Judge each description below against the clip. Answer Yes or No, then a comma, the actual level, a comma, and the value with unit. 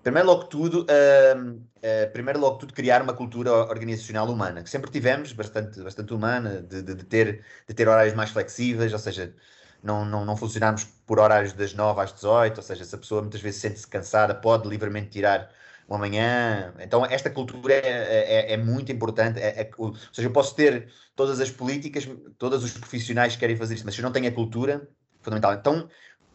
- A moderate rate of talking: No, fast, 200 wpm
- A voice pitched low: Yes, low, 115 Hz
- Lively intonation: No, average, 3.3 semitones